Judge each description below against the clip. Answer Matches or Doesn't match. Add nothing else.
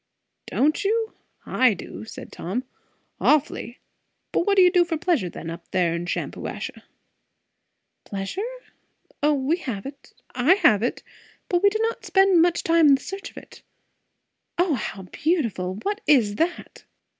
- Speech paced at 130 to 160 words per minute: Matches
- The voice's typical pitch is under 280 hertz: Doesn't match